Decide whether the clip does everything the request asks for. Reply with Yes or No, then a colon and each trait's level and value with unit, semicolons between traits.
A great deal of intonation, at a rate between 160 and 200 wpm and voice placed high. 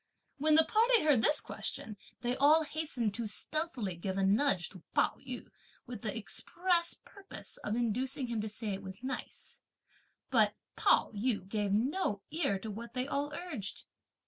Yes: wide, 6.5 semitones; average, 170 wpm; high, 245 Hz